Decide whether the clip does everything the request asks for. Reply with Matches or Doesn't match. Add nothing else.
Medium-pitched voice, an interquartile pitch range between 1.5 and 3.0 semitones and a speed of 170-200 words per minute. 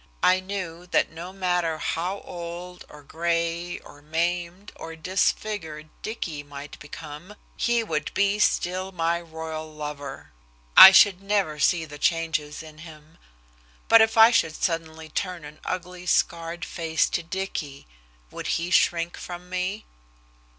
Doesn't match